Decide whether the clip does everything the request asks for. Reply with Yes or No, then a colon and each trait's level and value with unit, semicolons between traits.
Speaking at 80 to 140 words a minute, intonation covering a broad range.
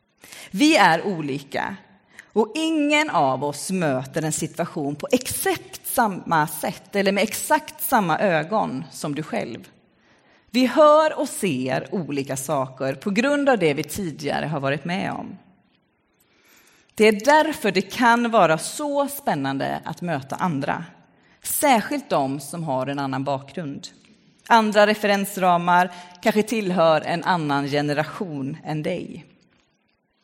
Yes: average, 130 wpm; wide, 7.9 semitones